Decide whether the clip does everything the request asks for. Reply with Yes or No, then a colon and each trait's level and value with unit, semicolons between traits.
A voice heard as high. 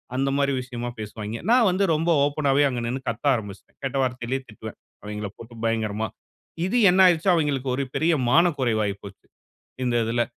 No: low, 125 Hz